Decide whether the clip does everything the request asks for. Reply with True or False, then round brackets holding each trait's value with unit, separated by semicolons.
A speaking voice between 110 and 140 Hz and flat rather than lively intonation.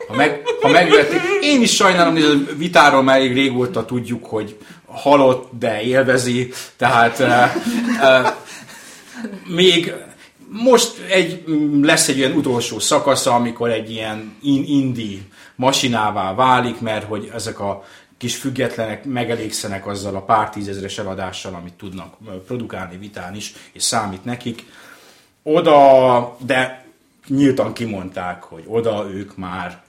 False (120 Hz; 5.0 semitones)